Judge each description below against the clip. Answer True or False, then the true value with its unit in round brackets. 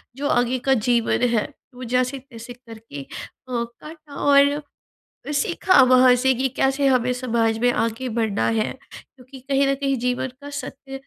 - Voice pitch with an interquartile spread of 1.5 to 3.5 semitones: True (2.6 semitones)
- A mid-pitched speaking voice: False (255 Hz)